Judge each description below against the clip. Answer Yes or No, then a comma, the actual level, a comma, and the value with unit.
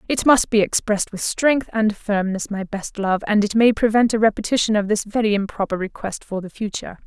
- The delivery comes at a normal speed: No, fast, 210 wpm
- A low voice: No, high, 210 Hz